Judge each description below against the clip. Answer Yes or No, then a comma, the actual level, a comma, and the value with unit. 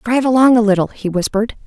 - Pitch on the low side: No, high, 225 Hz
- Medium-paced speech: No, fast, 215 wpm